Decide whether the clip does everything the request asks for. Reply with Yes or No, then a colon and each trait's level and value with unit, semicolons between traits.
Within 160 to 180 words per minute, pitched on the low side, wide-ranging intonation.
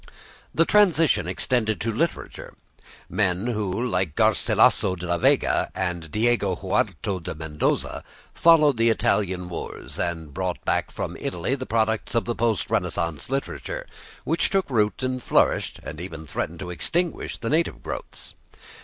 No: average, 145 wpm; low, 105 Hz; wide, 6.2 semitones